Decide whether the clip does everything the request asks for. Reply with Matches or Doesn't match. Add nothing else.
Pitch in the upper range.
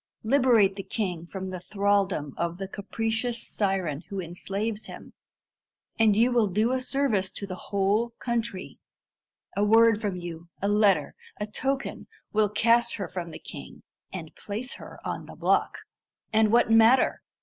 Matches